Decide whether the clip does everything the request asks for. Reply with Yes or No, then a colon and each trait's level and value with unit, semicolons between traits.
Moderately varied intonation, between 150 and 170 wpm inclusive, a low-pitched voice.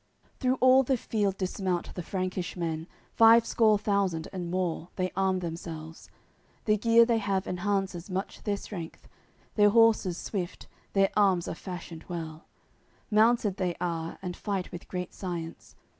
No: average, 3.1 semitones; average, 160 wpm; medium, 185 Hz